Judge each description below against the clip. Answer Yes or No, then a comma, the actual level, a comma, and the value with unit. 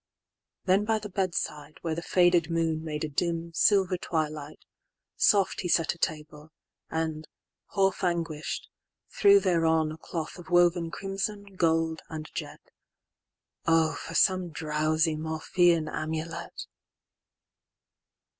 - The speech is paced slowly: Yes, slow, 110 wpm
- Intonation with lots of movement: No, narrow, 2.4 semitones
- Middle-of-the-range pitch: Yes, medium, 165 Hz